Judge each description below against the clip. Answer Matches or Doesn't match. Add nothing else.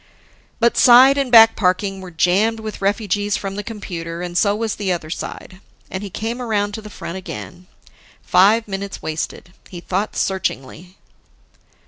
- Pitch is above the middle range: Matches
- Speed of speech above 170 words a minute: Doesn't match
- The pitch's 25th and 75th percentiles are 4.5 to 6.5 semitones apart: Doesn't match